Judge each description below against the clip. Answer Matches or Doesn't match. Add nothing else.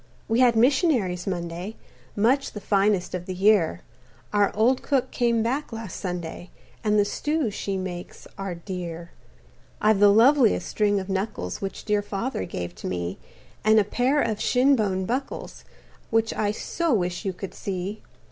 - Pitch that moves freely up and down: Doesn't match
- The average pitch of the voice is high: Matches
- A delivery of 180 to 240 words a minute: Doesn't match